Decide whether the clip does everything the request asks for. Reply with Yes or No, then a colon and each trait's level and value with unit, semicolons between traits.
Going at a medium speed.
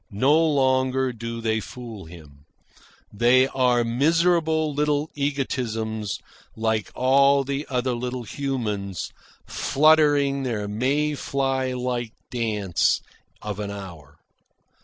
No: slow, 105 wpm